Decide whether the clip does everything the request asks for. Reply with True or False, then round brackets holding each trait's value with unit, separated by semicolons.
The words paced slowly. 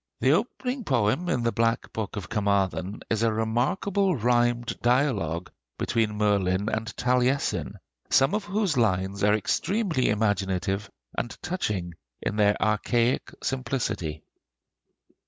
True (120 wpm)